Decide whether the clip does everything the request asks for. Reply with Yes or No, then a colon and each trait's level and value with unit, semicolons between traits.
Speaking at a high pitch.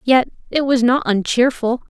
Yes: high, 245 Hz